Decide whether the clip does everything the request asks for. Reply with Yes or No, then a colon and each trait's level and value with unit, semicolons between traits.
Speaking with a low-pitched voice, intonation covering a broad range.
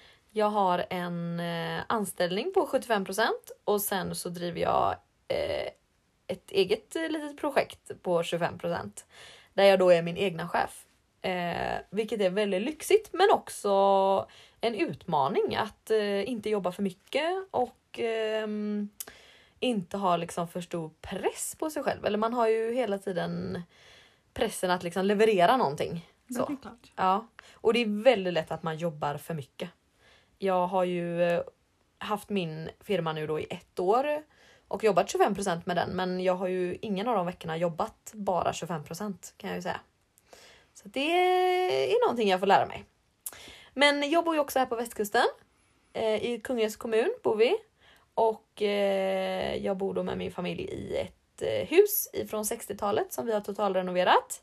No: high, 205 Hz; wide, 6.6 semitones